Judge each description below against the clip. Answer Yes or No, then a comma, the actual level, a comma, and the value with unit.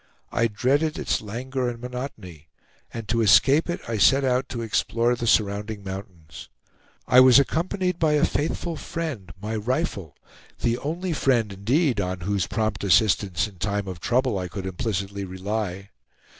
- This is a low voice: Yes, low, 110 Hz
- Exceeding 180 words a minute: No, average, 155 wpm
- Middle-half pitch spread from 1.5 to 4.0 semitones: No, average, 4.9 semitones